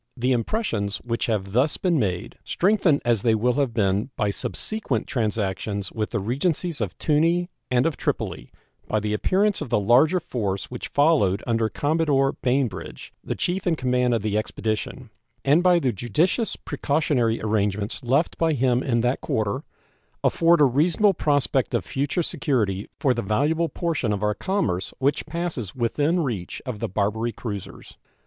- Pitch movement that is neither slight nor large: No, wide, 6.6 semitones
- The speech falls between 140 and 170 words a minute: Yes, average, 165 wpm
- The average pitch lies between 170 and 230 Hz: No, low, 125 Hz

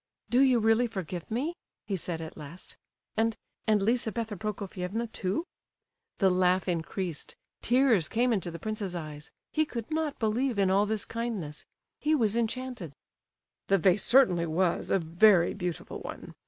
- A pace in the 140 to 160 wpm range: Yes, average, 145 wpm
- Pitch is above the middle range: Yes, high, 210 Hz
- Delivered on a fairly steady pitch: No, average, 4.7 semitones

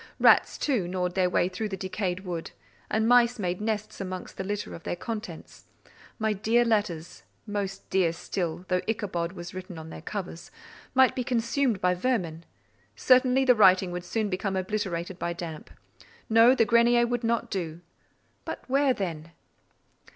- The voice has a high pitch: Yes, high, 195 Hz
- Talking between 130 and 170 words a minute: Yes, average, 160 wpm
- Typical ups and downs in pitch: Yes, average, 4.4 semitones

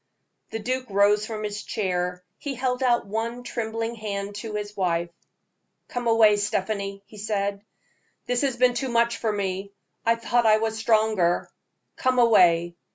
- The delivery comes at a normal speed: Yes, average, 160 wpm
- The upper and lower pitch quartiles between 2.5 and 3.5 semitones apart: Yes, average, 2.8 semitones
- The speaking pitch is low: No, high, 215 Hz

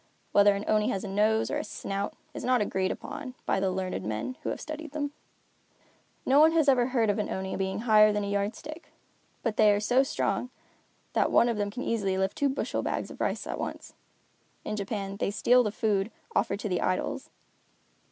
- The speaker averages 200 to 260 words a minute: Yes, fast, 205 wpm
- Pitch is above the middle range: Yes, high, 210 Hz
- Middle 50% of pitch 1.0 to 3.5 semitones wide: No, average, 3.9 semitones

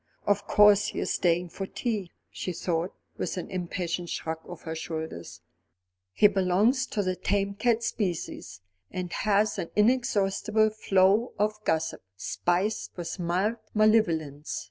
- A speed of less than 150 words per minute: Yes, average, 140 wpm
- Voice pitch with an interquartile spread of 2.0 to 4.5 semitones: Yes, average, 3.7 semitones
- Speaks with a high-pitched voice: Yes, high, 195 Hz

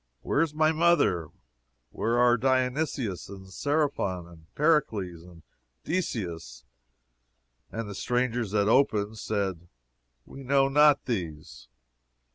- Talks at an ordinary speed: No, slow, 110 wpm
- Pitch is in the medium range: No, low, 115 Hz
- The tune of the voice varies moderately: No, wide, 7.2 semitones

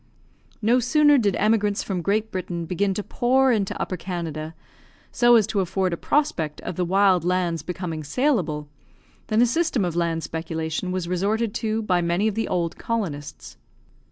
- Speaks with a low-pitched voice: No, medium, 185 Hz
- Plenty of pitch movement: No, average, 4.6 semitones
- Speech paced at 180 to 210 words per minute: No, average, 170 wpm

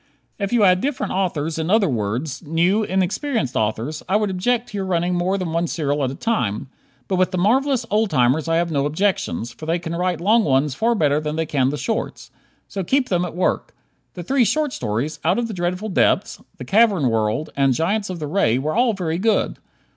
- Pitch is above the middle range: No, medium, 175 Hz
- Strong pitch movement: Yes, wide, 5.7 semitones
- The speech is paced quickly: Yes, fast, 220 wpm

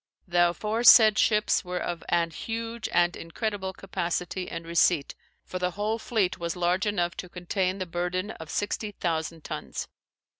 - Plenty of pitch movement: No, average, 3.1 semitones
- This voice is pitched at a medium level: Yes, medium, 180 Hz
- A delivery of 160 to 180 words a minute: No, average, 150 wpm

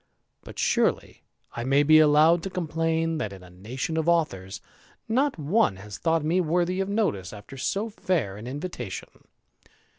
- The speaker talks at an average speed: Yes, average, 160 wpm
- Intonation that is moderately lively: No, wide, 7.2 semitones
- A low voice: No, medium, 155 Hz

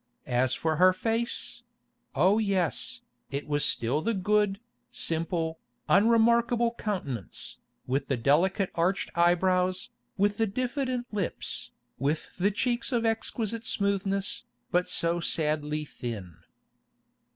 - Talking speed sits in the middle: No, slow, 110 wpm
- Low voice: No, high, 190 Hz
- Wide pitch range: Yes, wide, 6.1 semitones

